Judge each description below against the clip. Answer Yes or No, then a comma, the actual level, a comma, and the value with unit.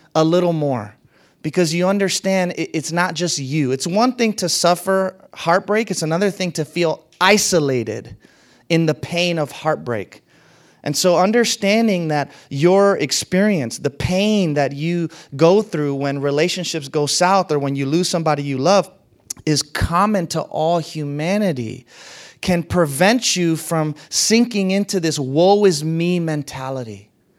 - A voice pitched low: No, medium, 165 Hz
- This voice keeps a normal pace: Yes, average, 145 wpm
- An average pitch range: Yes, average, 4.3 semitones